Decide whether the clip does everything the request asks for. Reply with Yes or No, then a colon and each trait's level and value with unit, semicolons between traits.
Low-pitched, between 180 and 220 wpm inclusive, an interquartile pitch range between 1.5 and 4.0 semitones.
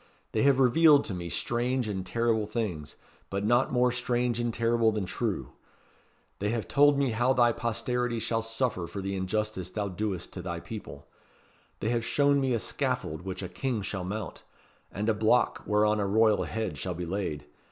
Yes: low, 110 Hz; average, 185 wpm; average, 3.7 semitones